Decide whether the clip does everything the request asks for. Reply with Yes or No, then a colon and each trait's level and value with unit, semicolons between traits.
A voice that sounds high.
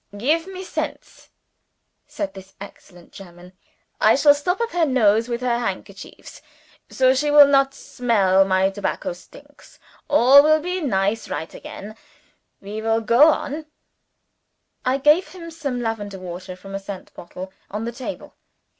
Yes: high, 235 Hz